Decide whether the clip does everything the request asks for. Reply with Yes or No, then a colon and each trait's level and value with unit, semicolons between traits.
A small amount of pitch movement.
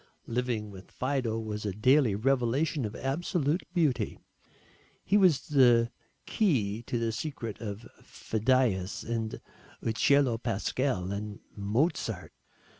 No: average, 4.4 semitones